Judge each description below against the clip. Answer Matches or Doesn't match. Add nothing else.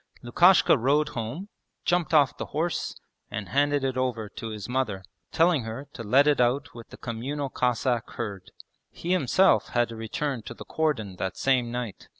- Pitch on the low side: Matches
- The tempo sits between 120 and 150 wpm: Doesn't match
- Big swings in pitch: Doesn't match